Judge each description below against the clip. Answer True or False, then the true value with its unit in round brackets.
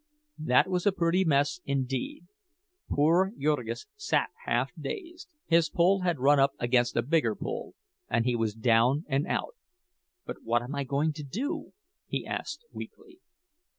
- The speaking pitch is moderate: True (150 Hz)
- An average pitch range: False (6.2 semitones)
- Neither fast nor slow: True (155 wpm)